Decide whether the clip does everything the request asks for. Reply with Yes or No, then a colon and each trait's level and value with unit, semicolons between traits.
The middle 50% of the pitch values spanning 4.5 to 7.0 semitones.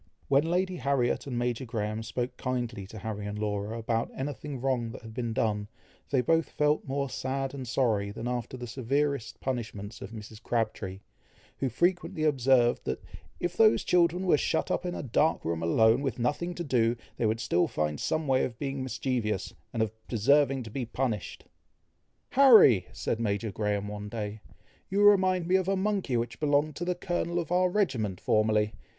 Yes: average, 5.2 semitones